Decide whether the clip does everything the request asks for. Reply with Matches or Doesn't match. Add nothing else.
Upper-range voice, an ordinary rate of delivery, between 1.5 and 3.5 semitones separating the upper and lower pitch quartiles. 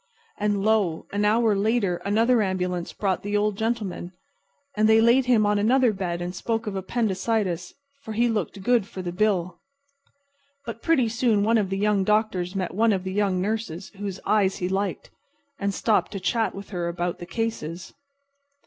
Matches